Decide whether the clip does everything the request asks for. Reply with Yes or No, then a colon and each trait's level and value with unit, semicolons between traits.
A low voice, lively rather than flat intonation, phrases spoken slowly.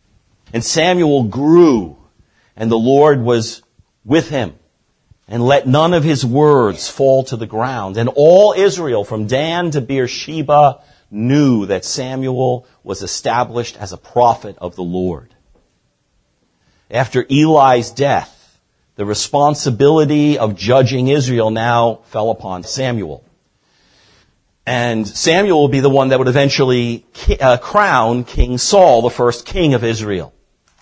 No: low, 125 Hz; average, 4.4 semitones; slow, 130 wpm